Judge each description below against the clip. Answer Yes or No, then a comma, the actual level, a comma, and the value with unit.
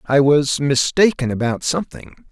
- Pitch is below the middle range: No, medium, 145 Hz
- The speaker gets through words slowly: Yes, slow, 130 wpm